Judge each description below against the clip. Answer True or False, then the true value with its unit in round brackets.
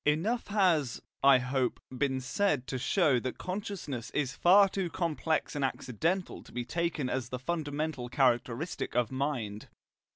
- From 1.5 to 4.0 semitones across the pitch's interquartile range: False (5.3 semitones)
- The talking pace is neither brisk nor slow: True (150 wpm)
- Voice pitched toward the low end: False (145 Hz)